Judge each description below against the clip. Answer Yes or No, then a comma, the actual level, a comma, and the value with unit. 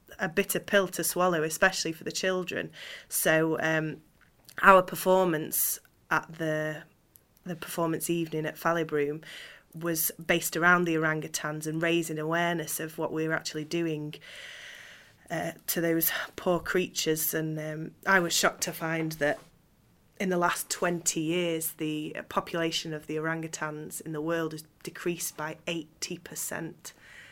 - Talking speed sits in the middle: Yes, average, 145 wpm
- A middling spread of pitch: No, narrow, 2.0 semitones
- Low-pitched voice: No, medium, 165 Hz